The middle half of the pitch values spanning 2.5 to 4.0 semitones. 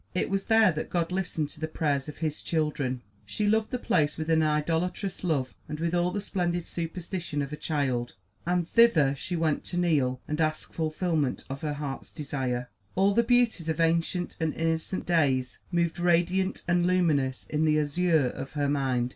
Yes: average, 3.4 semitones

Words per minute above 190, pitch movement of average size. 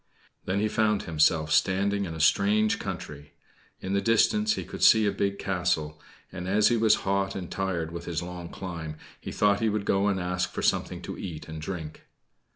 Yes: average, 200 wpm; average, 3.3 semitones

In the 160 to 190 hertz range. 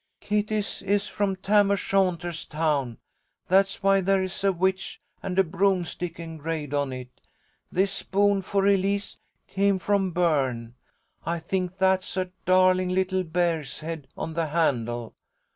Yes: medium, 185 Hz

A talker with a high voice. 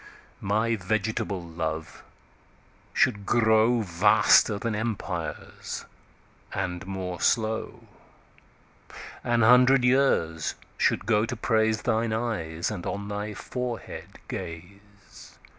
No: low, 105 Hz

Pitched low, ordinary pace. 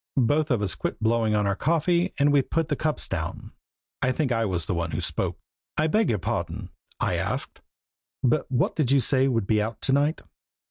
No: low, 130 Hz; fast, 215 wpm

